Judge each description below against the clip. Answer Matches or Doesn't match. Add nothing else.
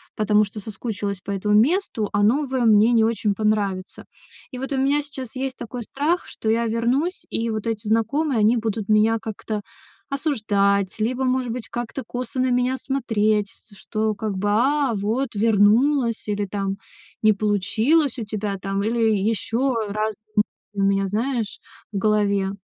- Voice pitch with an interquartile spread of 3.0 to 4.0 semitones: Matches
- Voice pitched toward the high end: Matches